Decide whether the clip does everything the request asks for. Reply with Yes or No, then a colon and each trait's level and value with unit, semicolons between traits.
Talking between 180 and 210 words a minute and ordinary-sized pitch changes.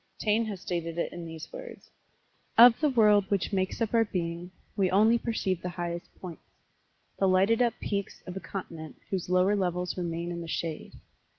Yes: average, 185 wpm; average, 3.5 semitones